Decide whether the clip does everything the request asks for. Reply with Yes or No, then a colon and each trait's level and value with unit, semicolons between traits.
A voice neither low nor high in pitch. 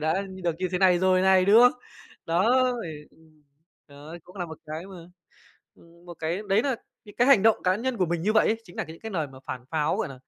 Yes: medium, 180 Hz